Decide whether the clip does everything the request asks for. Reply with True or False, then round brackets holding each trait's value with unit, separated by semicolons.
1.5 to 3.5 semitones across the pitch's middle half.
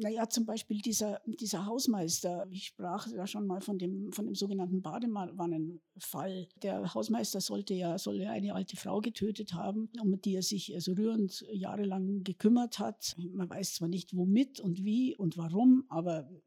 True (2.8 semitones)